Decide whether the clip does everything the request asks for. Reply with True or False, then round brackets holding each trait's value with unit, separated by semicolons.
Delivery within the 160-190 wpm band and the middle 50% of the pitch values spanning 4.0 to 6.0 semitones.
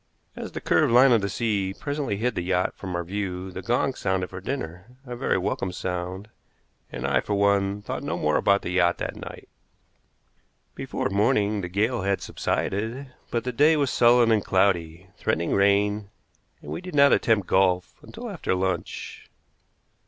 True (180 wpm; 4.4 semitones)